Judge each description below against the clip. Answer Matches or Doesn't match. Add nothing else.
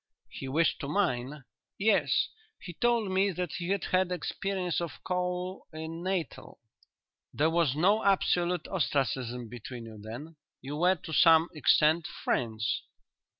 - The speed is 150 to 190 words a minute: Doesn't match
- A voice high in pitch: Doesn't match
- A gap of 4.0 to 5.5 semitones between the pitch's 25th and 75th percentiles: Matches